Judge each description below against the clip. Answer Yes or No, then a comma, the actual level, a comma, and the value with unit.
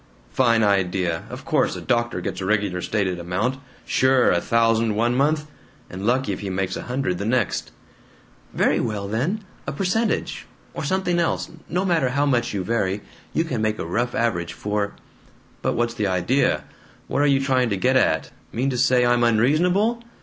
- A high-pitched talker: No, low, 120 Hz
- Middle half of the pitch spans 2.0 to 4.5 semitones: No, average, 5.1 semitones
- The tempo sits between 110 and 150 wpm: No, average, 185 wpm